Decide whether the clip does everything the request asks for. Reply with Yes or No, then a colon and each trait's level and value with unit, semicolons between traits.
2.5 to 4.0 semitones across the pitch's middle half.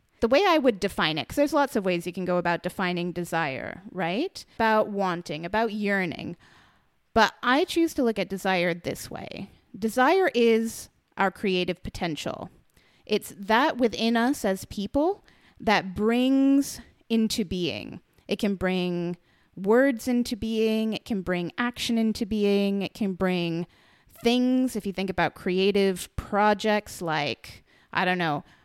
No: average, 4.4 semitones